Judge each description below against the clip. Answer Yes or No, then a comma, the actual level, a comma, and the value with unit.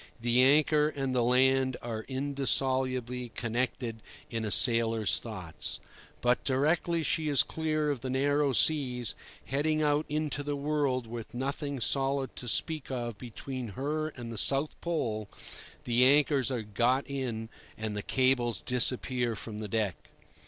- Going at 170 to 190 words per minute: No, average, 145 wpm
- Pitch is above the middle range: No, low, 130 Hz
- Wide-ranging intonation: No, average, 3.3 semitones